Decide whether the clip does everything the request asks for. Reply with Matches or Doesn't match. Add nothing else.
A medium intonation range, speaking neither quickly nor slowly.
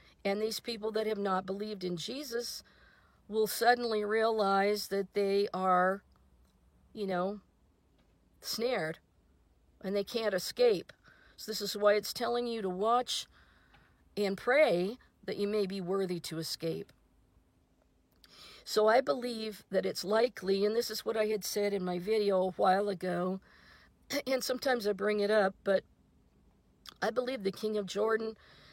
Matches